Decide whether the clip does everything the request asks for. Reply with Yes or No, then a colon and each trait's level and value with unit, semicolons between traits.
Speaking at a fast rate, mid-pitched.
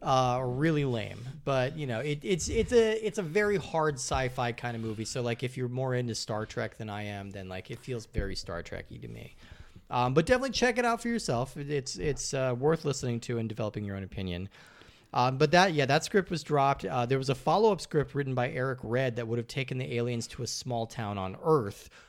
No: fast, 235 wpm; low, 130 Hz